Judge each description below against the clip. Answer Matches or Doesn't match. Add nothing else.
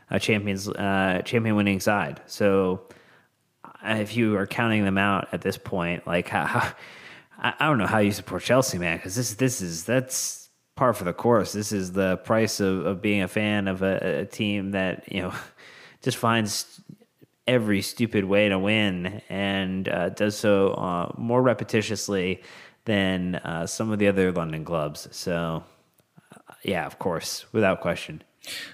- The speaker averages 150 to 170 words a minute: Matches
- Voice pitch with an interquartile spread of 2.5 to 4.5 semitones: Matches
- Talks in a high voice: Doesn't match